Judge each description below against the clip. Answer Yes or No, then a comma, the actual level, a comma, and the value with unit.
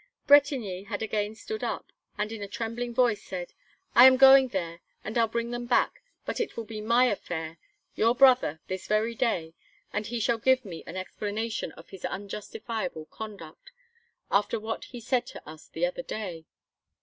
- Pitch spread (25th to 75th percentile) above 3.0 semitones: Yes, average, 3.6 semitones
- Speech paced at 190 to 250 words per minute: No, average, 180 wpm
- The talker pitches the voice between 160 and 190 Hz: No, high, 220 Hz